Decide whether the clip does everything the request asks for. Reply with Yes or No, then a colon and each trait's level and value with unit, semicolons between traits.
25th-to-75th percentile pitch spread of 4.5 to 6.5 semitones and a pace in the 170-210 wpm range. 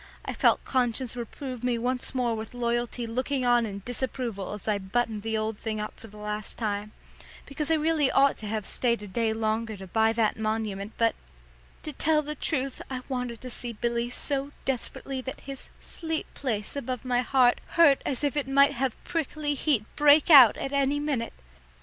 No: average, 3.7 semitones; average, 190 wpm